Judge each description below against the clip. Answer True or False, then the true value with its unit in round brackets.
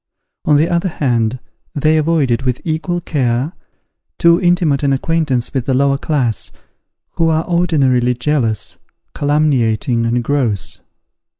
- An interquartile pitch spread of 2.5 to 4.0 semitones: False (4.5 semitones)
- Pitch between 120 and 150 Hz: True (140 Hz)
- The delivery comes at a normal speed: False (125 wpm)